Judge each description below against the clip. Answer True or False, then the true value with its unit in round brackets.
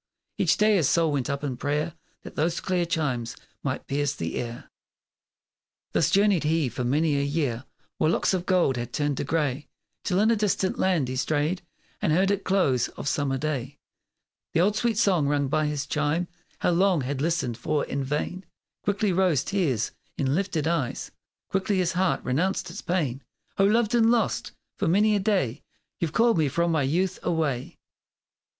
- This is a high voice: False (160 Hz)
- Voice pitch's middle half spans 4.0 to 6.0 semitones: True (5.1 semitones)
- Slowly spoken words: False (185 wpm)